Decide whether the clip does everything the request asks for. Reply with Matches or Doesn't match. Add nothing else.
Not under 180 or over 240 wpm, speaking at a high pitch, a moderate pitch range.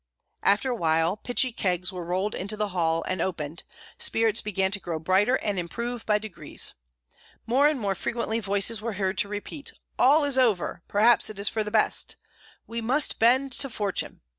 Matches